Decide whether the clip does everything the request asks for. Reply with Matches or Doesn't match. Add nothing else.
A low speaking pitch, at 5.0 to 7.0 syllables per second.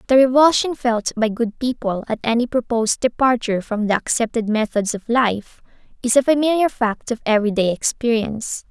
Doesn't match